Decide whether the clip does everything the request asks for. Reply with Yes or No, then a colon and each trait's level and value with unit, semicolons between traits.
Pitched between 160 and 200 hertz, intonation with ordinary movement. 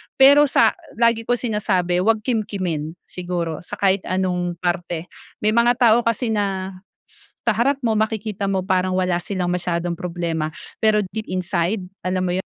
Yes: high, 190 Hz; average, 3.7 semitones